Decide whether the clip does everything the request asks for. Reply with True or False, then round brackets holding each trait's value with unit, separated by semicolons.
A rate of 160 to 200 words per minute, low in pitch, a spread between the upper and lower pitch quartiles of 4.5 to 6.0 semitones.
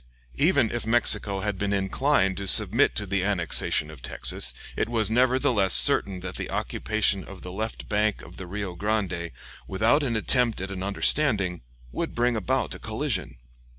False (170 wpm; 105 Hz; 3.8 semitones)